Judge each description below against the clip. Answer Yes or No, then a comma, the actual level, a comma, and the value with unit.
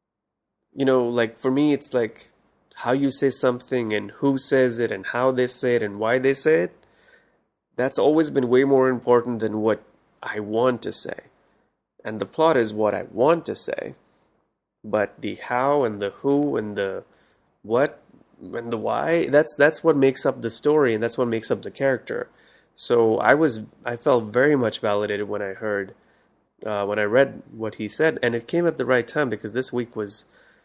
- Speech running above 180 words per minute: Yes, average, 195 wpm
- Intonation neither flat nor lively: Yes, average, 4.0 semitones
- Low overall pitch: Yes, low, 120 Hz